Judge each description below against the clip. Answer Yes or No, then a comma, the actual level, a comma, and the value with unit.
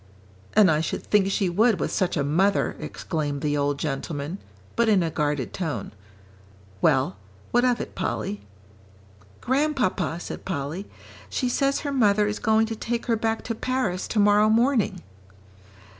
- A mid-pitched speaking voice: No, high, 200 Hz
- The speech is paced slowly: No, average, 155 wpm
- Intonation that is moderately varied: No, wide, 6.4 semitones